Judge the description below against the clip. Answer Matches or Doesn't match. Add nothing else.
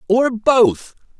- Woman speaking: Doesn't match